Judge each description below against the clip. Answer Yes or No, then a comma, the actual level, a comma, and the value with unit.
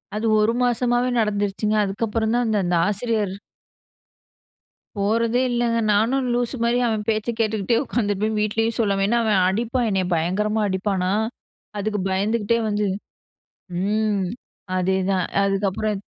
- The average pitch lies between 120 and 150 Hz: No, high, 215 Hz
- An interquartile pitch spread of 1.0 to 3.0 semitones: Yes, narrow, 2.6 semitones